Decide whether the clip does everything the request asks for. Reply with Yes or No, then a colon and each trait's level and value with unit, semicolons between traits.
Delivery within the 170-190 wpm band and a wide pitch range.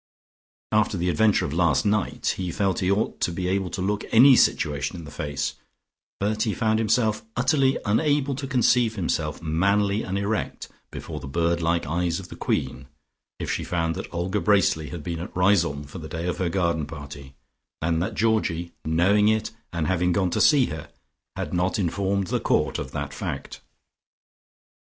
No: average, 185 wpm; average, 4.3 semitones